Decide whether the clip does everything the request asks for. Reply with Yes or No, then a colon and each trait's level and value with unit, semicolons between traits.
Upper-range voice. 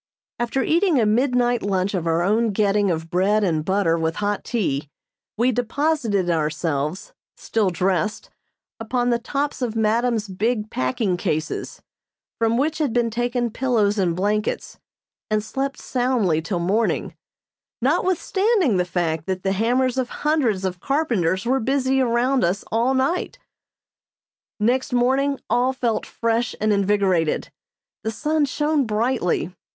Yes: high, 225 Hz